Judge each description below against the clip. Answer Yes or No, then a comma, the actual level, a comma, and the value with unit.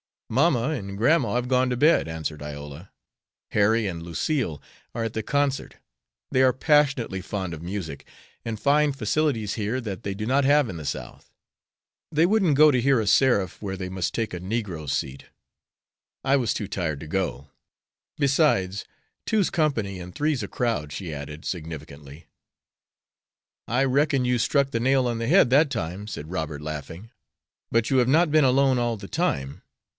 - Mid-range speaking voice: No, low, 115 Hz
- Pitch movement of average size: No, wide, 7.4 semitones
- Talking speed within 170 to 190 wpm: Yes, average, 175 wpm